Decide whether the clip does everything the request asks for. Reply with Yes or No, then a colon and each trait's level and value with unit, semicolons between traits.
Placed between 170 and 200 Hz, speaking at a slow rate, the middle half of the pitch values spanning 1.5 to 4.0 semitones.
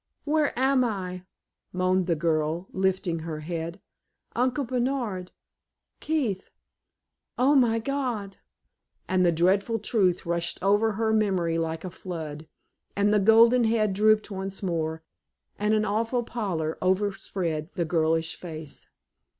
No: high, 190 Hz; slow, 125 wpm; average, 4.8 semitones